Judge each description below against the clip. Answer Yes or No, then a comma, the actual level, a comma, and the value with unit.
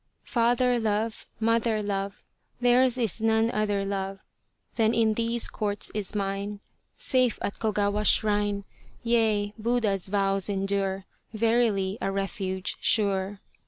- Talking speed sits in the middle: No, slow, 120 wpm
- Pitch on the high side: Yes, high, 210 Hz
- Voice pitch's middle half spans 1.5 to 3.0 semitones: Yes, narrow, 2.5 semitones